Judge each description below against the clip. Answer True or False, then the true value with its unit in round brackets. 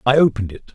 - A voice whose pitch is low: True (115 Hz)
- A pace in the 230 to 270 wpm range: True (240 wpm)